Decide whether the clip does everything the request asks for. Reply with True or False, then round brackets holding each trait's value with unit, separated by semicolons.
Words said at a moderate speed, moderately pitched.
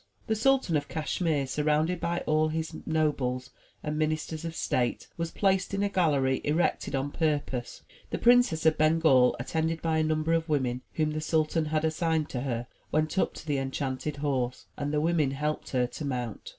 True (185 wpm; 155 Hz)